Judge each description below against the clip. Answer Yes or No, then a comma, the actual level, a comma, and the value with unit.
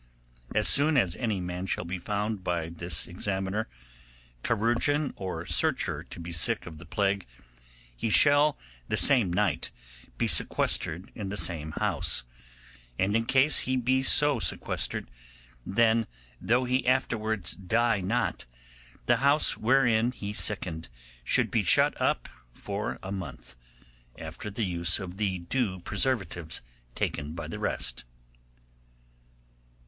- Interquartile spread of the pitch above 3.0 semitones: Yes, average, 5.3 semitones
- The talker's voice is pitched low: Yes, low, 105 Hz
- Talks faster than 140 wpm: No, slow, 135 wpm